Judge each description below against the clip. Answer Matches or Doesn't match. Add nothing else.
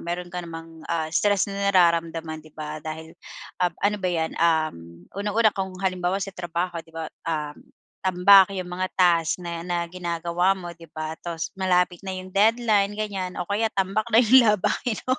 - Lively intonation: Doesn't match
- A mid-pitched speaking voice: Matches